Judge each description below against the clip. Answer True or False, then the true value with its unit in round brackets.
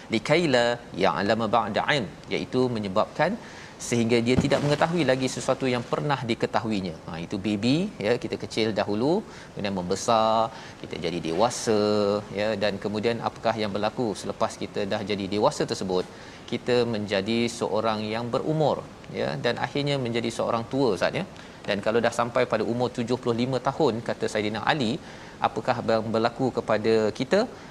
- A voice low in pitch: True (115 Hz)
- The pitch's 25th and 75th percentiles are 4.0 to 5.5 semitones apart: False (2.8 semitones)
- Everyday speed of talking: False (145 wpm)